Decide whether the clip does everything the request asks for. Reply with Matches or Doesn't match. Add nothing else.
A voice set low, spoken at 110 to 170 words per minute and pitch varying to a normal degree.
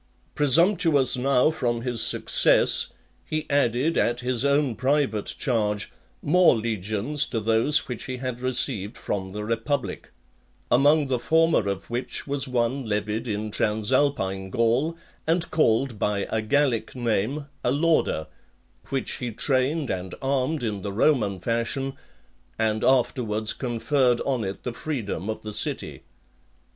Matches